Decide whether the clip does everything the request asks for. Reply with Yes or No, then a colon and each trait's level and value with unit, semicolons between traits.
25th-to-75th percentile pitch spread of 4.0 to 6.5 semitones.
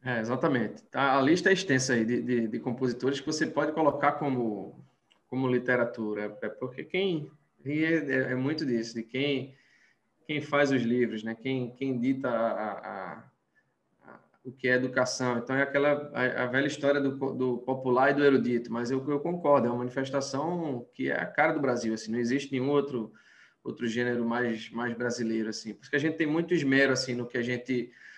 No: average, 2.9 semitones